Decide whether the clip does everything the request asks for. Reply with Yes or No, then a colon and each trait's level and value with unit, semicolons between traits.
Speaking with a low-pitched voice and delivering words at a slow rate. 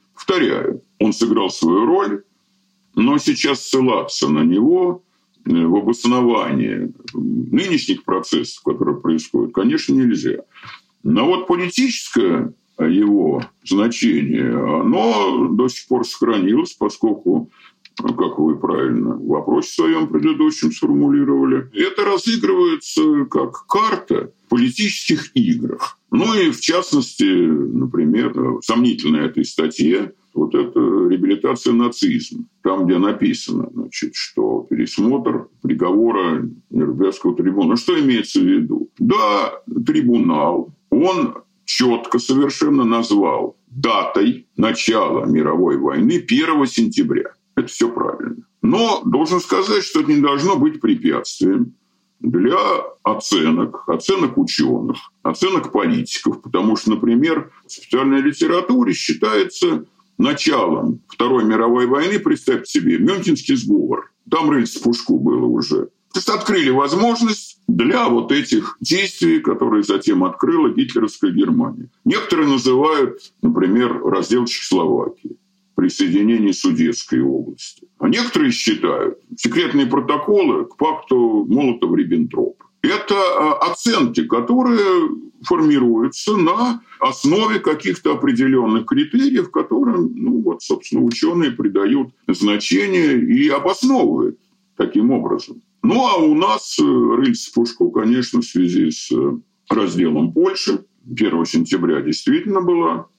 No: very high, 295 Hz; slow, 105 wpm